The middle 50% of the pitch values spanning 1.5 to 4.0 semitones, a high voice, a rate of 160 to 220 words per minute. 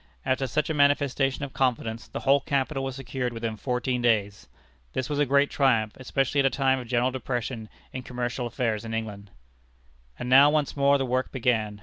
No: average, 2.8 semitones; low, 130 Hz; average, 195 wpm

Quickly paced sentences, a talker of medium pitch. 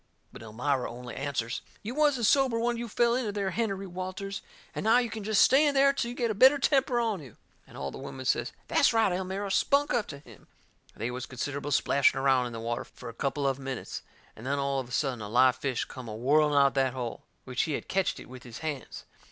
Yes: fast, 245 wpm; medium, 145 Hz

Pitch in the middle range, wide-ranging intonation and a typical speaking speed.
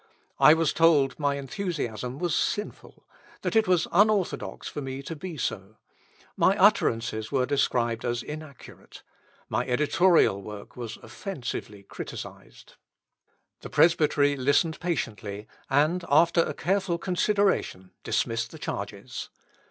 No: medium, 145 Hz; wide, 6.3 semitones; slow, 120 wpm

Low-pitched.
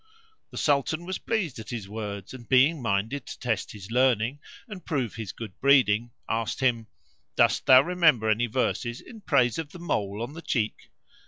Yes: low, 125 Hz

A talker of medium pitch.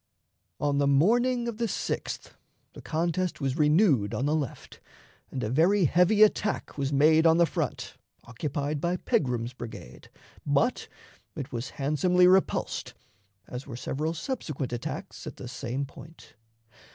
Yes: medium, 150 Hz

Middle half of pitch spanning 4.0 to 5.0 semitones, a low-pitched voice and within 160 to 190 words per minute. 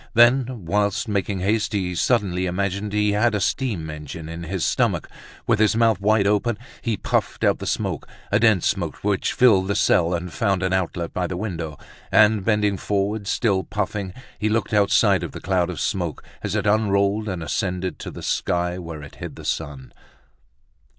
No: average, 3.0 semitones; low, 100 Hz; average, 185 wpm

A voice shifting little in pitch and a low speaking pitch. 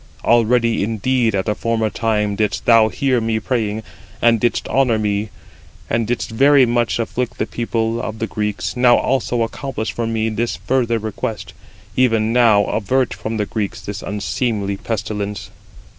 Yes: narrow, 1.9 semitones; low, 115 Hz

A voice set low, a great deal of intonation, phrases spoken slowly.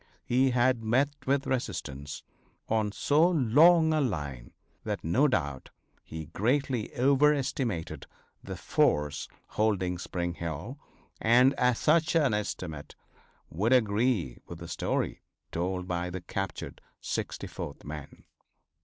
Yes: low, 110 Hz; wide, 7.8 semitones; slow, 115 wpm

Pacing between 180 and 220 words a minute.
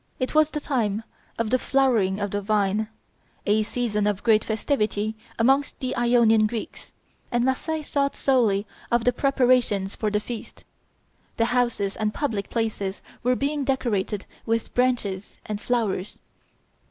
No: average, 145 wpm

